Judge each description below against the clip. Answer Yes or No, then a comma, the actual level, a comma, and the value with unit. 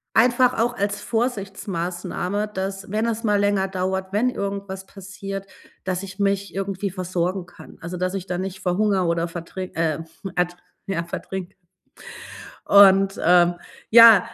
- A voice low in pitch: No, high, 195 Hz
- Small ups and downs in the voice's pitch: Yes, narrow, 1.8 semitones